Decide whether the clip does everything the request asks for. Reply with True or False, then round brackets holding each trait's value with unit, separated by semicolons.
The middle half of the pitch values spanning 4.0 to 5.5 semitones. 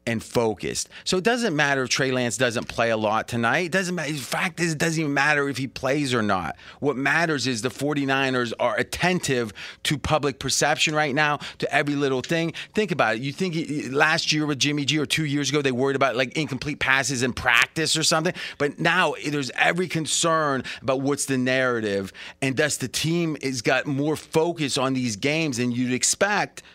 False (3.5 semitones)